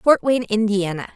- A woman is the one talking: Yes, female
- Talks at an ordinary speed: Yes, average, 155 wpm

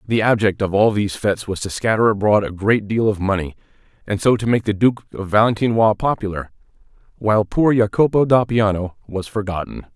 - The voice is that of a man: Yes, male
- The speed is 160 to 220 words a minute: Yes, average, 180 wpm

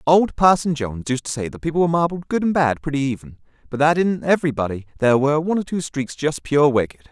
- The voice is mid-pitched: Yes, medium, 145 Hz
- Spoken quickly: Yes, fast, 235 wpm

